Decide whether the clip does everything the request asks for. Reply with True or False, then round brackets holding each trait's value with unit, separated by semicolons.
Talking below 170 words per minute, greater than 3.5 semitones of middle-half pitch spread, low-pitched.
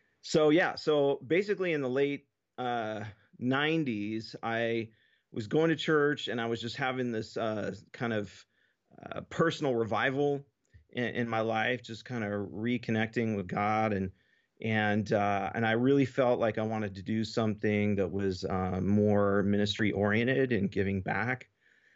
True (160 wpm; 3.9 semitones; 115 Hz)